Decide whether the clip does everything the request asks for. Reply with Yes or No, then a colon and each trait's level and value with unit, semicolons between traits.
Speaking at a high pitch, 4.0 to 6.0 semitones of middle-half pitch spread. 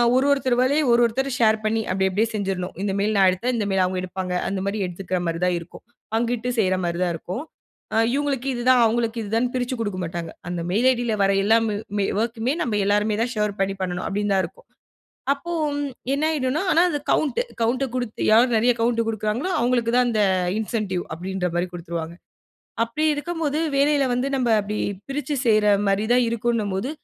Yes: high, 220 Hz; average, 4.5 semitones